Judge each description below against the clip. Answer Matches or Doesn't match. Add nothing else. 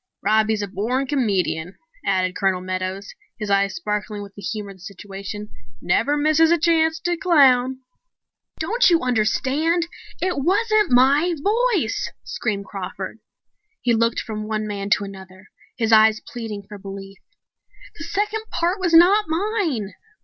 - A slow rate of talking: Doesn't match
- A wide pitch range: Matches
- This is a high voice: Matches